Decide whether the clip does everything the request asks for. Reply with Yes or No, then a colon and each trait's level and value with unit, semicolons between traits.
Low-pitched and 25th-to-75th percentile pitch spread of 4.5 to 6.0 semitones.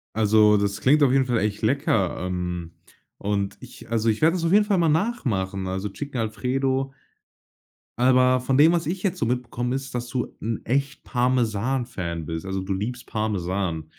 Yes: low, 120 Hz; average, 5.2 semitones